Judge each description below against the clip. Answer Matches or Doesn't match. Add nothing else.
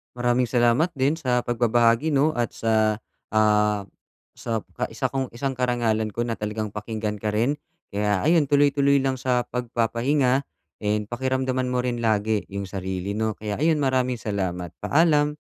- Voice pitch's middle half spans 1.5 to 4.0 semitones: Matches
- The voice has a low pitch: Matches